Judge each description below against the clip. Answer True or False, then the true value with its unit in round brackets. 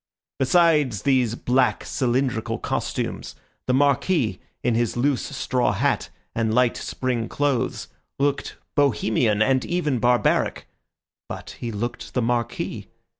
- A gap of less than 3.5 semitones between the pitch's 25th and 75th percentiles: True (2.8 semitones)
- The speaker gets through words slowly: True (120 wpm)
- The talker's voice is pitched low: True (125 Hz)